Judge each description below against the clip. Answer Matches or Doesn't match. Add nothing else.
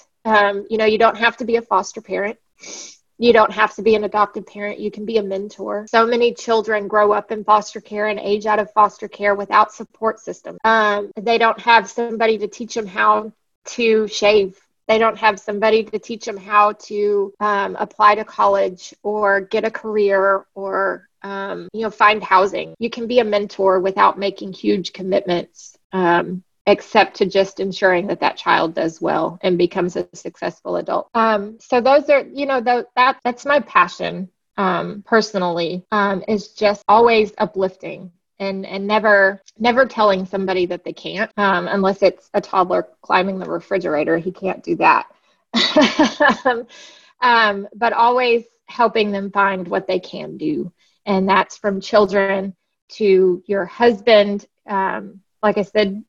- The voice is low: Doesn't match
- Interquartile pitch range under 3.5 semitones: Matches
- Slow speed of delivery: Doesn't match